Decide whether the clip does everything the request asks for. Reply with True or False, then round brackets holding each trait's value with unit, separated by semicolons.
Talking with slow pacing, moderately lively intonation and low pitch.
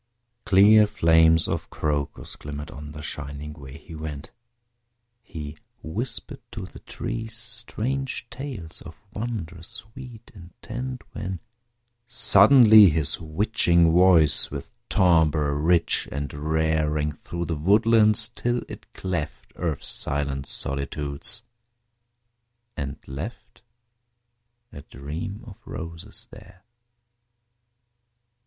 False (105 wpm; 6.5 semitones; 85 Hz)